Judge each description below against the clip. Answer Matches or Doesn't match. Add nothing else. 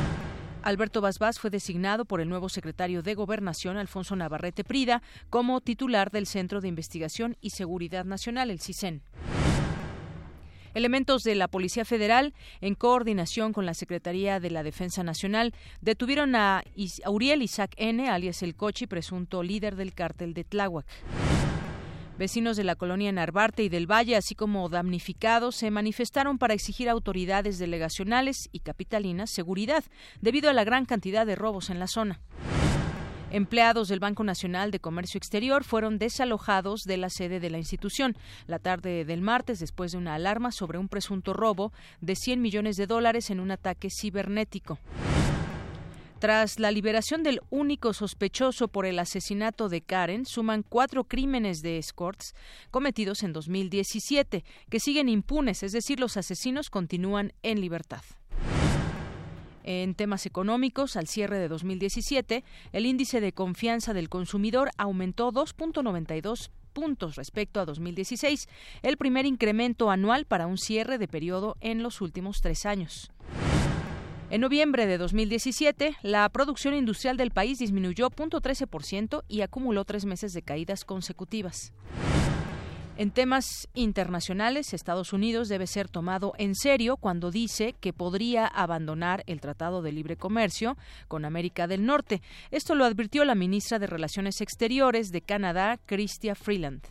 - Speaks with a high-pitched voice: Matches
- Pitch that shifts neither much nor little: Matches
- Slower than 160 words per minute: Matches